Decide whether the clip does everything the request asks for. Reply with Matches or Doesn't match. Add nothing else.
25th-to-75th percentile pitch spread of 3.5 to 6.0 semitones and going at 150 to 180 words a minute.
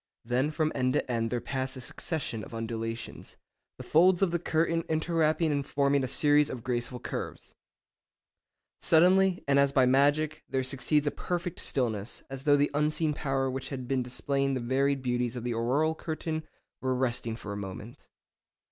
Matches